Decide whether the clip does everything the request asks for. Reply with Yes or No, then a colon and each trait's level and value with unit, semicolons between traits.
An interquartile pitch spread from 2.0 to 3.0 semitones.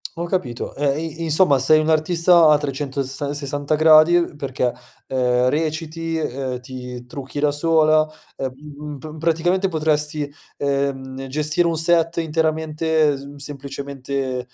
Yes: average, 2.7 semitones